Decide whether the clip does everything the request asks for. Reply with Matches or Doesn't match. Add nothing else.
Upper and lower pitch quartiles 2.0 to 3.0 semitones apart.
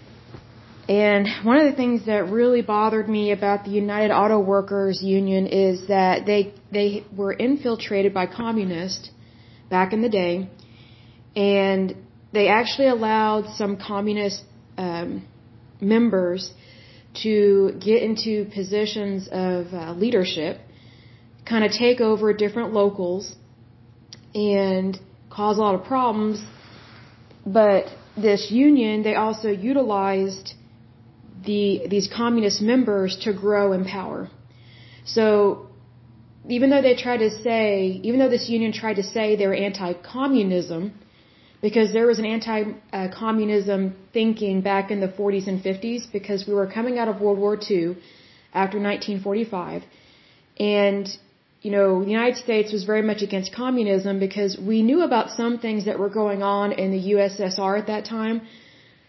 Matches